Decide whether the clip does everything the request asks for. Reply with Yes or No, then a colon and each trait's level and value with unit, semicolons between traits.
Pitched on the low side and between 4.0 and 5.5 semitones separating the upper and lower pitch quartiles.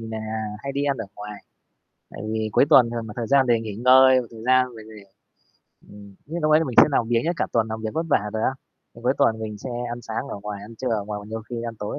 No: low, 115 Hz; average, 3.0 semitones